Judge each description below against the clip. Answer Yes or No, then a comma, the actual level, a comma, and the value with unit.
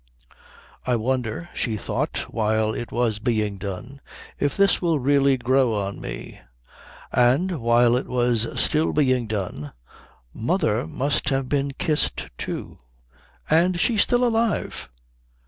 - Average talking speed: No, slow, 130 wpm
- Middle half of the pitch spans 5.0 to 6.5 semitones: No, average, 4.6 semitones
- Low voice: Yes, low, 125 Hz